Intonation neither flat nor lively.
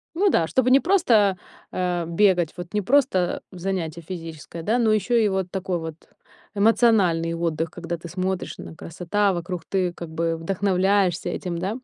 Yes: average, 3.3 semitones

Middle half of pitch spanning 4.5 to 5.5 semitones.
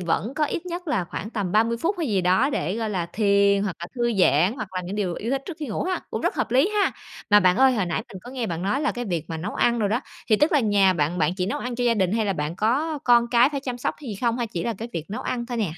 Yes: average, 5.2 semitones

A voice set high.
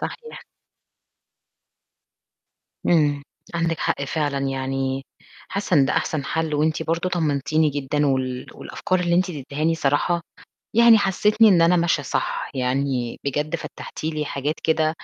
No: medium, 155 Hz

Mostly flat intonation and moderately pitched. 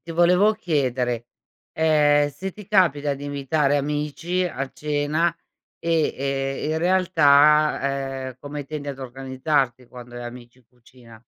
No: average, 3.2 semitones; medium, 145 Hz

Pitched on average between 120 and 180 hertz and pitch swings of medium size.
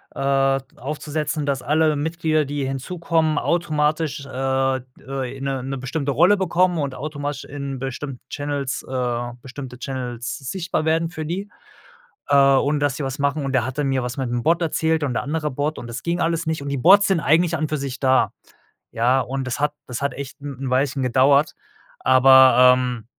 Yes: medium, 140 Hz; average, 3.0 semitones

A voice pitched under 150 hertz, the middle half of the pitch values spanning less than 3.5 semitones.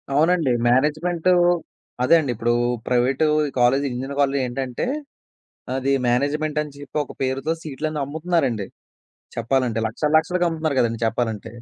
No: medium, 140 Hz; average, 4.0 semitones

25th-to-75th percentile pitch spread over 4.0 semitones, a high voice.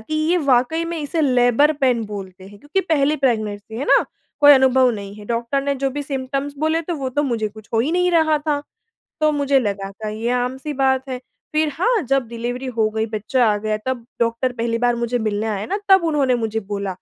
Yes: average, 4.6 semitones; very high, 255 Hz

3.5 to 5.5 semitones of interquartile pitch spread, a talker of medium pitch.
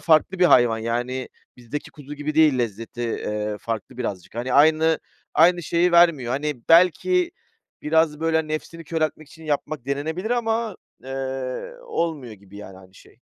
Yes: average, 5.2 semitones; medium, 150 Hz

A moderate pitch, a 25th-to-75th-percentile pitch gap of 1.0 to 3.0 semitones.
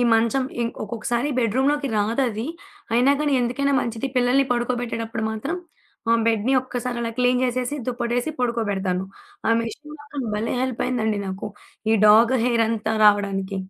No: high, 235 Hz; narrow, 2.5 semitones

